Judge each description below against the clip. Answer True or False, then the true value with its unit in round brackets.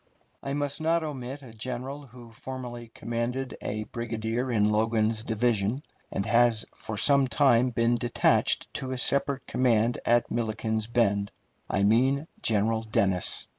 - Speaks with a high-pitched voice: False (120 Hz)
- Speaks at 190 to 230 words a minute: False (140 wpm)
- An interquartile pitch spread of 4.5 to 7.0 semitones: False (2.8 semitones)